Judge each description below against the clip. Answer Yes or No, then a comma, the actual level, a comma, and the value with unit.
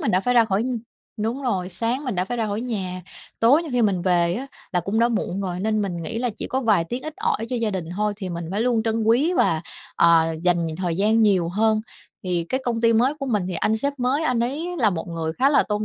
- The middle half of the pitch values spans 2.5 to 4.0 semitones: No, average, 5.2 semitones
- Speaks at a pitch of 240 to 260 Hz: No, high, 220 Hz